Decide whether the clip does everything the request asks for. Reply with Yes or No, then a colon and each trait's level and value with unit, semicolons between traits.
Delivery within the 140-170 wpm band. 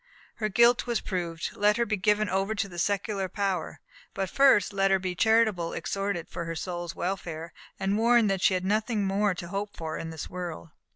No: fast, 205 wpm